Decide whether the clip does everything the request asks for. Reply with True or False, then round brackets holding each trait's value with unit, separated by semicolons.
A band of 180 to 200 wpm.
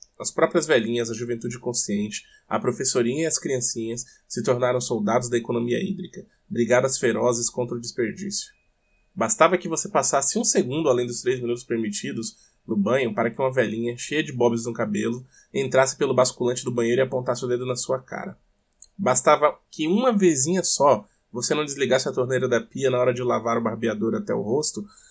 True (185 wpm)